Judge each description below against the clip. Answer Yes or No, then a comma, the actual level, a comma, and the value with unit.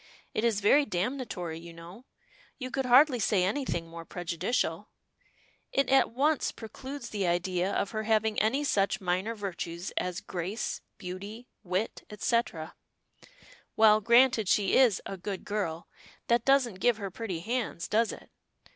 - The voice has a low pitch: No, high, 210 Hz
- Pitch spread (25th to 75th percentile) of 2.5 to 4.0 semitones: No, average, 4.8 semitones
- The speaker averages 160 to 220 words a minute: No, average, 145 wpm